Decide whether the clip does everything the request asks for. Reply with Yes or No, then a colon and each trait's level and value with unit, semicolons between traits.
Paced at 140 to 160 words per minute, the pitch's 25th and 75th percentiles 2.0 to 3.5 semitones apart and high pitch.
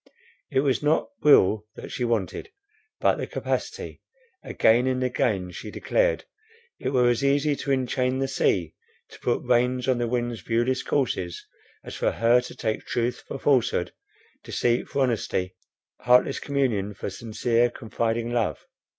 No: average, 150 wpm; narrow, 2.4 semitones; low, 120 Hz